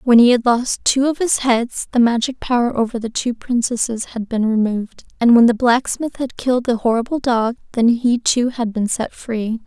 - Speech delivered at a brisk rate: Yes, fast, 210 wpm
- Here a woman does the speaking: Yes, female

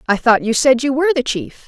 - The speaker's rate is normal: No, fast, 285 wpm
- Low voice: No, very high, 260 Hz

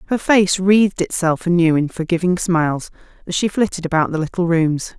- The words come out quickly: No, average, 180 wpm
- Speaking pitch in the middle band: Yes, medium, 175 Hz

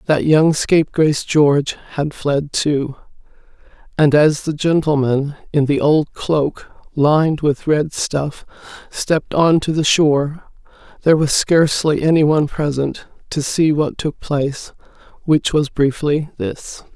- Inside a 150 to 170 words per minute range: No, average, 140 wpm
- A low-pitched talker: No, medium, 150 Hz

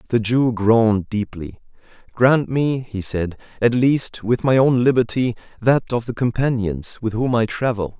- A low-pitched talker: Yes, low, 115 Hz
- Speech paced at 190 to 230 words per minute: No, average, 160 wpm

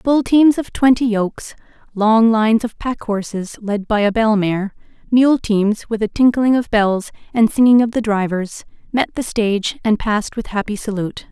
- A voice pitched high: Yes, high, 220 Hz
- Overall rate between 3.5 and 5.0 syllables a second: Yes, 4.7 syllables/s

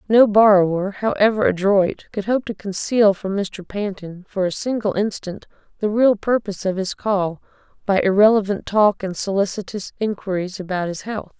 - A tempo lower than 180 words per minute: Yes, average, 160 wpm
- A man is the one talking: No, female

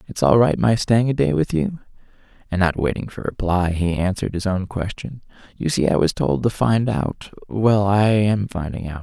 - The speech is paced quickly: Yes, fast, 215 wpm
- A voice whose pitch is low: Yes, low, 100 Hz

